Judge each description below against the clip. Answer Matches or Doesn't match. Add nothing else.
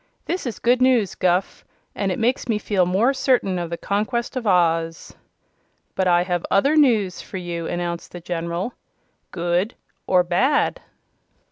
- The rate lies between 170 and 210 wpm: Doesn't match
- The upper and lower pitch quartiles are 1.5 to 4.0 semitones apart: Doesn't match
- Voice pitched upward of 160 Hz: Matches